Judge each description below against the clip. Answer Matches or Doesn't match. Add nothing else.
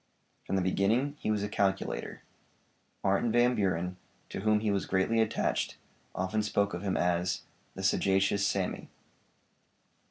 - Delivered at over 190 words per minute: Doesn't match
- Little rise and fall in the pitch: Matches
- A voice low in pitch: Matches